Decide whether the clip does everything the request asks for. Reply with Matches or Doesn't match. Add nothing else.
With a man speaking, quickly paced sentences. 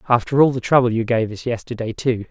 Matches